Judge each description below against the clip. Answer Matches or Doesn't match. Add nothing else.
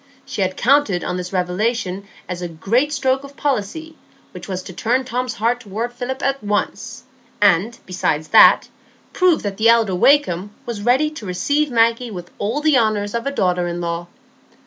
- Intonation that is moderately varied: Doesn't match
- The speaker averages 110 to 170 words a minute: Doesn't match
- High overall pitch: Matches